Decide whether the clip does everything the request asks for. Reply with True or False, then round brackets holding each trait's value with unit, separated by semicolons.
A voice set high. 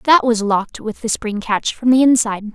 True (230 Hz)